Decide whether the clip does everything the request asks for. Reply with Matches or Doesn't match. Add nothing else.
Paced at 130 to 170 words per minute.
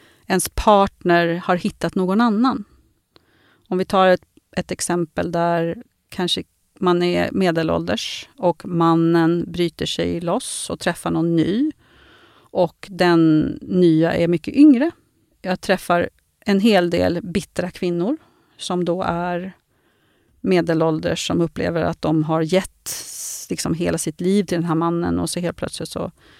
Matches